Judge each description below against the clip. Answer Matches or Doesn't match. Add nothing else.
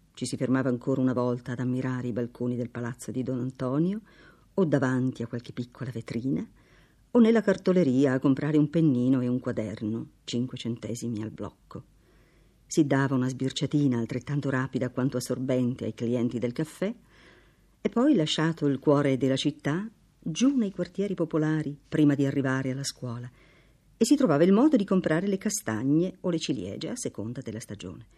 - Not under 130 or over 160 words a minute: Doesn't match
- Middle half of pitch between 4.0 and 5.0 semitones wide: Matches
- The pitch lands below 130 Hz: Doesn't match